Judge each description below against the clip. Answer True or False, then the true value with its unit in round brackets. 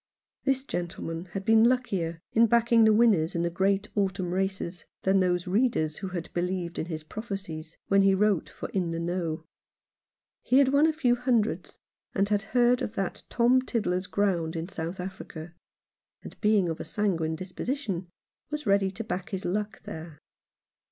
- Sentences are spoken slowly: False (170 wpm)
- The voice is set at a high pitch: True (195 Hz)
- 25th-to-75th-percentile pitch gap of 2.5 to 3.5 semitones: False (4.5 semitones)